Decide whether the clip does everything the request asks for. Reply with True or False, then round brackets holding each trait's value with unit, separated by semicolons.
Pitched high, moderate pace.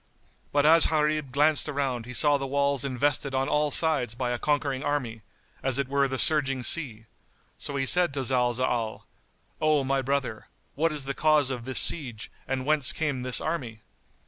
False (135 Hz; 180 wpm)